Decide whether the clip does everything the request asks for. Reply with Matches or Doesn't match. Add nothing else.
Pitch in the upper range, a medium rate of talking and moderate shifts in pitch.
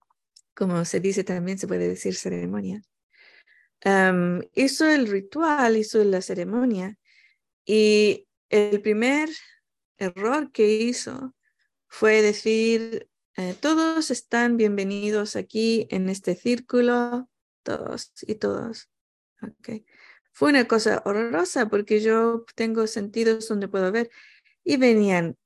Doesn't match